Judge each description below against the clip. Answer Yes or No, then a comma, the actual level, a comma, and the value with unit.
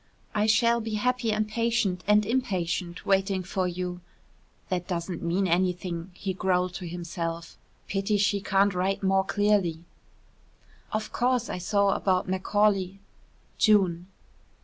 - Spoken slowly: Yes, slow, 130 wpm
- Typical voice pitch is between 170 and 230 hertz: Yes, high, 190 Hz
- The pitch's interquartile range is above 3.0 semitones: No, average, 2.7 semitones